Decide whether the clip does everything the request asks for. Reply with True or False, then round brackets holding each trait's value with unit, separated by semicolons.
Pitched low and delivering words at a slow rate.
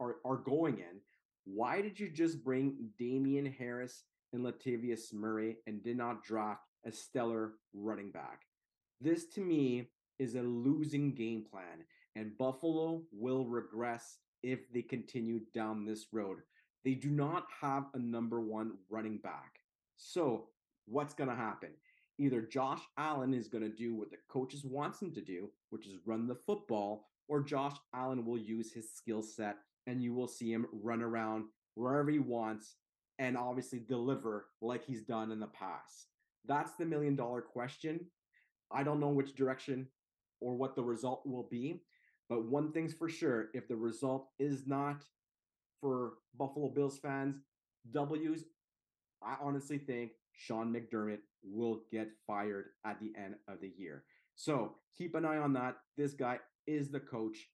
False (125 Hz; 160 wpm)